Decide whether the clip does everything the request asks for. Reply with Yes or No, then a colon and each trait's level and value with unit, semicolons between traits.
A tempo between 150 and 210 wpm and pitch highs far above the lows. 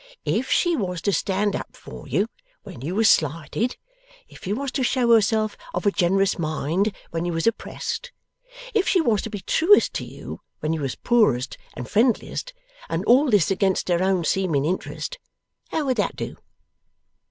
Yes: average, 180 wpm; wide, 5.7 semitones